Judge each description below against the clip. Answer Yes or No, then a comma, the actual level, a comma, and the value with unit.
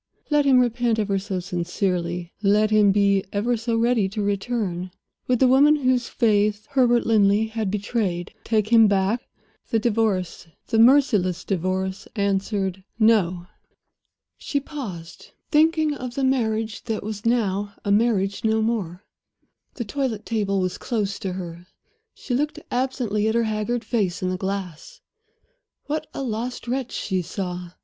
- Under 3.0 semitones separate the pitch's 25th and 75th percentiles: No, average, 3.9 semitones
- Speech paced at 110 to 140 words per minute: No, average, 150 wpm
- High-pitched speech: Yes, high, 215 Hz